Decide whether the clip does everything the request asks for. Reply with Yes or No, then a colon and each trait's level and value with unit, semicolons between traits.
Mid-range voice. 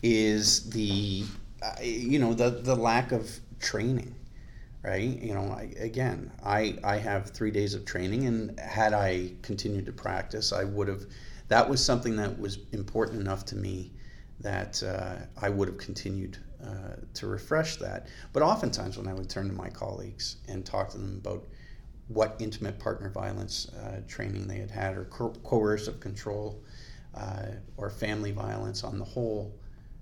No: low, 105 Hz